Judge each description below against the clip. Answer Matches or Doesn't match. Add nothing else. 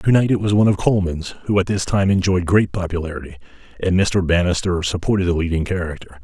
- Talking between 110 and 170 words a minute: Doesn't match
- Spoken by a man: Matches